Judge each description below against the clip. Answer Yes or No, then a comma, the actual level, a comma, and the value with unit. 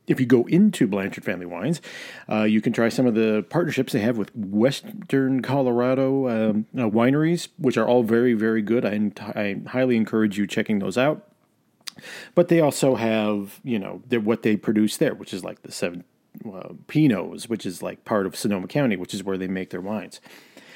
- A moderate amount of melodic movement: Yes, average, 3.3 semitones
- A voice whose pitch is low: Yes, low, 115 Hz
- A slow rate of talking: No, average, 195 wpm